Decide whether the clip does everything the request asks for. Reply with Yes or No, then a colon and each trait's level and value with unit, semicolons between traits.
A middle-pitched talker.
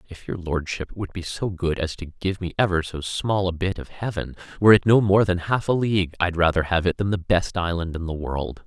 No: very low, 90 Hz